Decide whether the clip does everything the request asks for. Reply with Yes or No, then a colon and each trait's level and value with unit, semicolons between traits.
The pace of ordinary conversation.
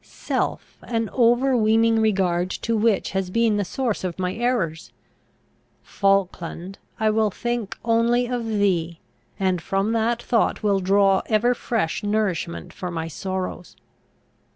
No: slow, 130 wpm